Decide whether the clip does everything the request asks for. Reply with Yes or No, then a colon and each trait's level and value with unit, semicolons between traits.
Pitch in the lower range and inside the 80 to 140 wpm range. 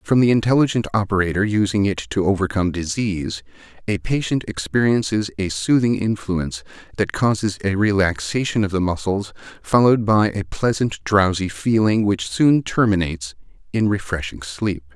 Yes: low, 100 Hz; slow, 135 wpm